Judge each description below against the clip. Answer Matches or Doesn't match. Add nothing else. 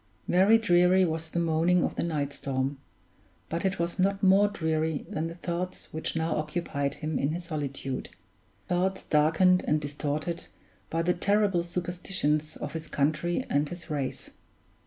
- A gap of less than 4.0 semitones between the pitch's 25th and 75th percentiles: Matches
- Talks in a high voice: Doesn't match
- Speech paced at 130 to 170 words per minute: Matches